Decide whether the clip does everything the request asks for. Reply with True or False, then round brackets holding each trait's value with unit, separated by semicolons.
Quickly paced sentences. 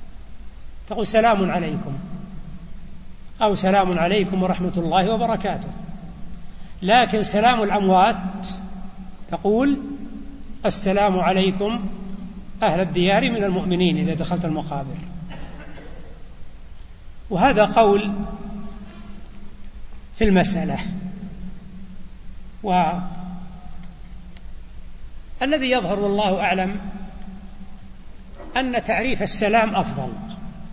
False (65 wpm)